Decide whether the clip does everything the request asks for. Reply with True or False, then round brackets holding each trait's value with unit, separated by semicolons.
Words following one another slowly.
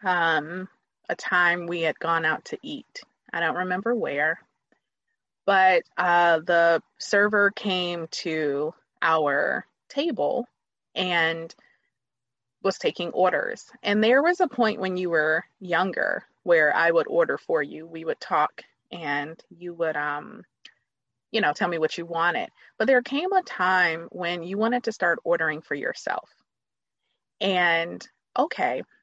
False (145 wpm)